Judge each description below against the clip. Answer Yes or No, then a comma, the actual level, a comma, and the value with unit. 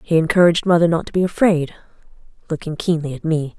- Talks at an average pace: Yes, average, 185 wpm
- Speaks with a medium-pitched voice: Yes, medium, 165 Hz